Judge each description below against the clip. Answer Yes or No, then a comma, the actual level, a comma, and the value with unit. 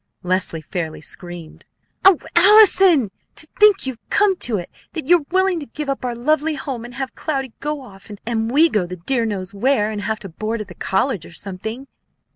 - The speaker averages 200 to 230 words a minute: Yes, fast, 205 wpm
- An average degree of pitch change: No, wide, 7.5 semitones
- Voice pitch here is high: Yes, high, 240 Hz